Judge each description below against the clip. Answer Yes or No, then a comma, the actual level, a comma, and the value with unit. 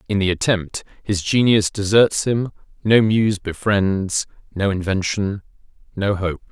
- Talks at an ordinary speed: No, slow, 130 wpm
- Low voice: Yes, low, 100 Hz